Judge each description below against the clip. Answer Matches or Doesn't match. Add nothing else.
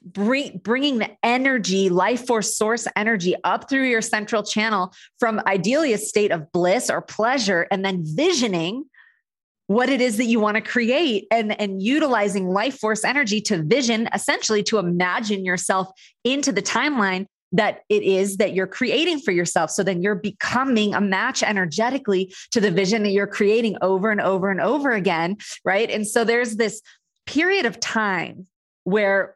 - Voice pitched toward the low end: Doesn't match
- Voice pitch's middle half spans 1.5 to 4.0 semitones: Matches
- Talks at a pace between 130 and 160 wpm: Doesn't match